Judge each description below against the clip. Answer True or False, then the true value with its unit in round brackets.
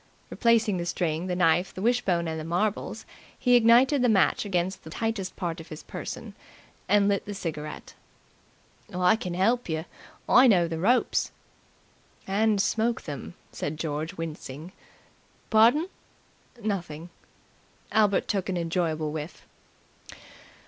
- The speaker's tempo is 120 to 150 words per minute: True (135 wpm)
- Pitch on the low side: False (185 Hz)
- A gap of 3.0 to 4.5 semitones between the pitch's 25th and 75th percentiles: False (5.0 semitones)